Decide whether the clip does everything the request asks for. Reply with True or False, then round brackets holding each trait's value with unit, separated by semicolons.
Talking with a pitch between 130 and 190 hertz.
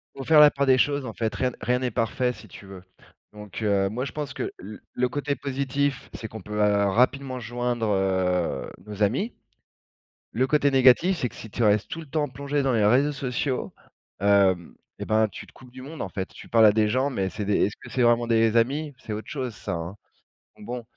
False (120 Hz)